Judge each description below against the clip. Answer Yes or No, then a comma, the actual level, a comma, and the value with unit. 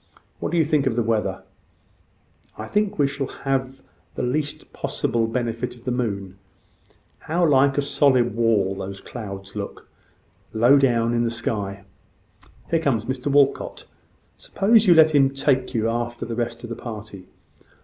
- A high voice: No, low, 120 Hz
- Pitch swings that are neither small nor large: Yes, average, 3.6 semitones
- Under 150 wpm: No, average, 160 wpm